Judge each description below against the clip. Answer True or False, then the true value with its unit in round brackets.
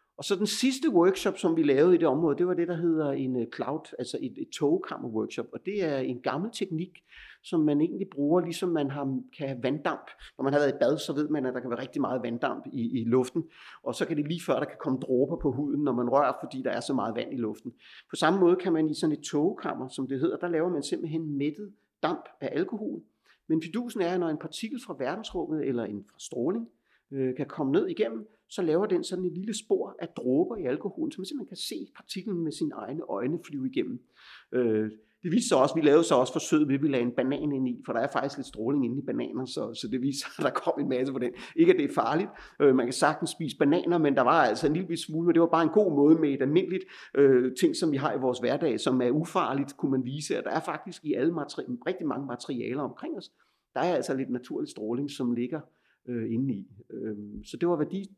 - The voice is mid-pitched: True (155 Hz)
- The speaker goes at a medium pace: False (250 wpm)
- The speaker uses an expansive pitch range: True (6.0 semitones)